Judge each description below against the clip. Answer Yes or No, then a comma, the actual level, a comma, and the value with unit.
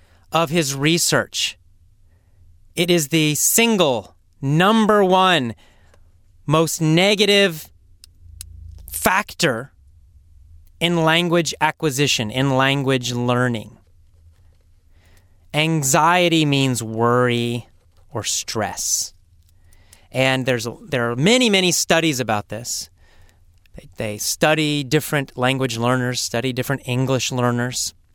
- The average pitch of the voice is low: Yes, low, 120 Hz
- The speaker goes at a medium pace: No, slow, 90 wpm